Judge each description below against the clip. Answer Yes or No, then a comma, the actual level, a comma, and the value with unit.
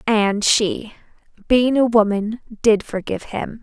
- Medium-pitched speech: No, high, 220 Hz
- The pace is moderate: No, slow, 130 wpm